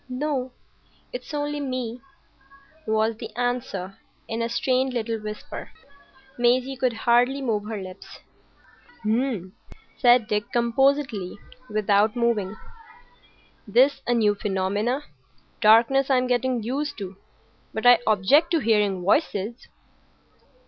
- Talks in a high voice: Yes, high, 235 Hz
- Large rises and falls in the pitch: No, average, 3.4 semitones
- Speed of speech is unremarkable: No, slow, 115 wpm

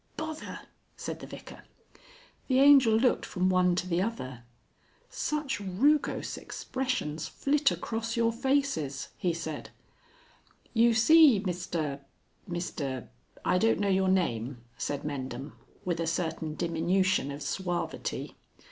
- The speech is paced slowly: Yes, slow, 120 wpm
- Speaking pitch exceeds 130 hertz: Yes, medium, 185 Hz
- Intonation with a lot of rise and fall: Yes, wide, 6.8 semitones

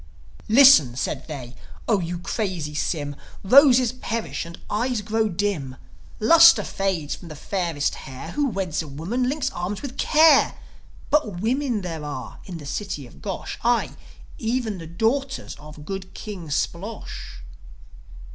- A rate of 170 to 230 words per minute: No, average, 145 wpm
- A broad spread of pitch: Yes, wide, 7.0 semitones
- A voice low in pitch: No, high, 195 Hz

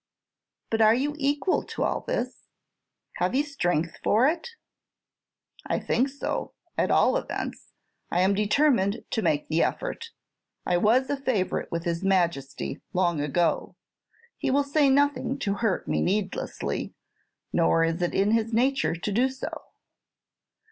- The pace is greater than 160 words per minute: No, average, 150 wpm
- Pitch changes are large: Yes, wide, 7.5 semitones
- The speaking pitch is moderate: No, high, 215 Hz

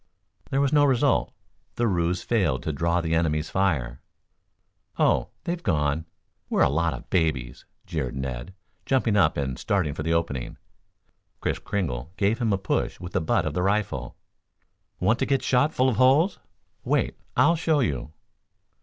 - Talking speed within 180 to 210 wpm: No, average, 165 wpm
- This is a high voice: No, very low, 90 Hz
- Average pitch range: No, wide, 7.7 semitones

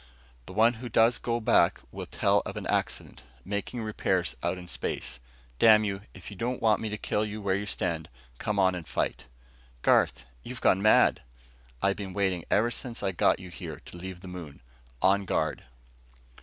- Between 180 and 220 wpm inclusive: Yes, average, 185 wpm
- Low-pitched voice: Yes, low, 100 Hz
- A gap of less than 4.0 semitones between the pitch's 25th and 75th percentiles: Yes, average, 3.1 semitones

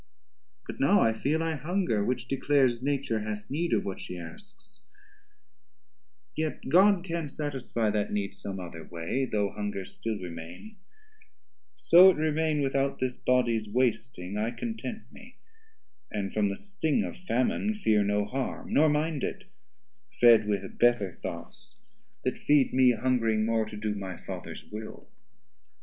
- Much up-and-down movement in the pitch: Yes, wide, 6.9 semitones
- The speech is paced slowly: No, average, 150 wpm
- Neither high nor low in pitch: No, low, 125 Hz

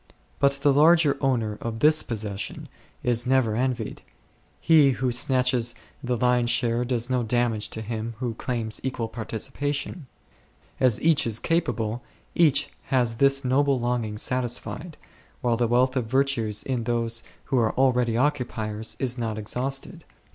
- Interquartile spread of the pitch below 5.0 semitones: Yes, average, 2.8 semitones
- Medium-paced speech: Yes, average, 145 wpm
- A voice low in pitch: Yes, low, 125 Hz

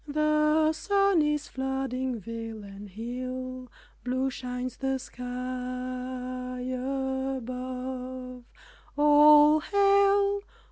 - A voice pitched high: Yes, very high, 255 Hz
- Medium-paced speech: No, slow, 80 wpm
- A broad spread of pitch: No, average, 2.9 semitones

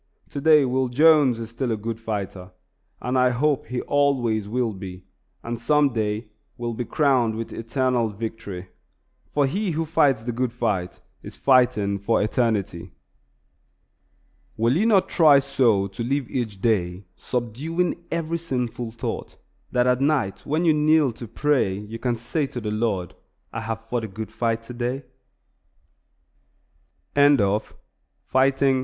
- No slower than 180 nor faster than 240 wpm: No, average, 150 wpm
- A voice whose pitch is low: Yes, low, 120 Hz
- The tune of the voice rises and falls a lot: No, average, 3.9 semitones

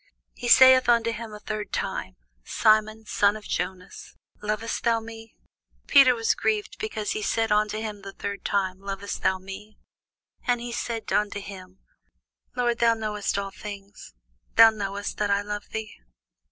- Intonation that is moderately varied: No, narrow, 2.1 semitones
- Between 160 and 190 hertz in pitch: No, high, 215 Hz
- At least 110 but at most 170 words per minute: Yes, average, 160 wpm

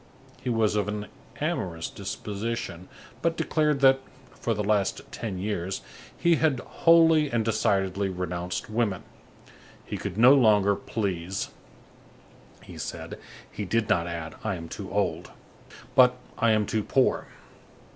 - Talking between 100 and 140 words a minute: Yes, slow, 135 wpm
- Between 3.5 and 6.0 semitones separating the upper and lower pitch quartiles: Yes, average, 4.0 semitones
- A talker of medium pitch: No, low, 105 Hz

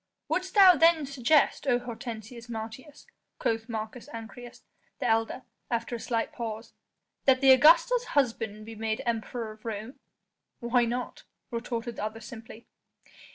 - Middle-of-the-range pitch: No, high, 235 Hz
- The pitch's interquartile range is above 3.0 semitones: No, average, 2.7 semitones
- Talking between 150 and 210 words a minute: No, average, 140 wpm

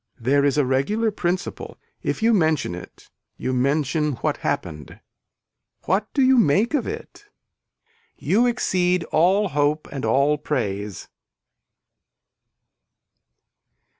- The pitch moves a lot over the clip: Yes, wide, 7.4 semitones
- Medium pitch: Yes, medium, 155 Hz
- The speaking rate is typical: No, slow, 110 wpm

